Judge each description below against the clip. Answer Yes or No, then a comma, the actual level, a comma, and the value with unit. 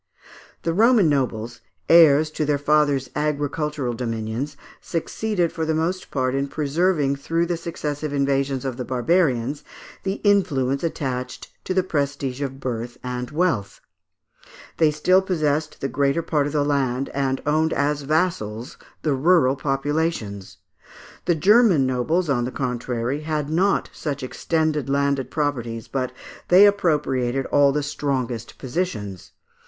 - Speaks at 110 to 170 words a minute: Yes, average, 140 wpm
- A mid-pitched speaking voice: Yes, medium, 145 Hz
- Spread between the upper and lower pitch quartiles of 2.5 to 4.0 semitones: Yes, average, 3.6 semitones